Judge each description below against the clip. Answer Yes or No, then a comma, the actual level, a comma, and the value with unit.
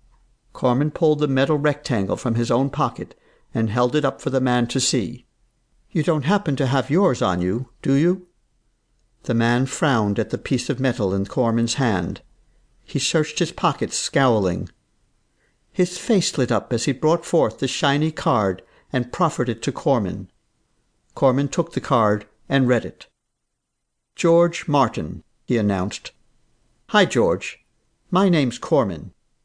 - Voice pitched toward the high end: No, low, 130 Hz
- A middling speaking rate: Yes, average, 155 wpm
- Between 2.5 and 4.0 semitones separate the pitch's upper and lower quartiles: No, average, 4.4 semitones